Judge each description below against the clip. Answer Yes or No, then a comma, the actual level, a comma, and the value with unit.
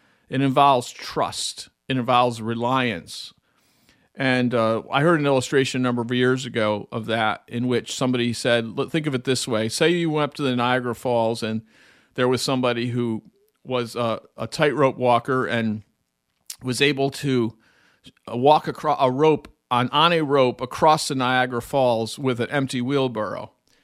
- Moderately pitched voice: No, low, 125 Hz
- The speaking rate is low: No, average, 165 wpm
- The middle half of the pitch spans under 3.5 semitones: Yes, average, 2.7 semitones